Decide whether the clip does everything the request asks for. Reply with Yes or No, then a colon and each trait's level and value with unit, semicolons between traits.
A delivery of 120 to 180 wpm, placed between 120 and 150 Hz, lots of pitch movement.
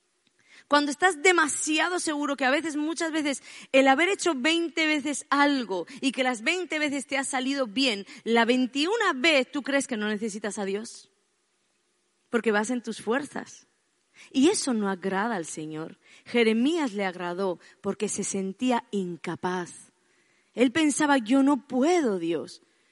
No: average, 150 wpm; very high, 265 Hz; wide, 6.2 semitones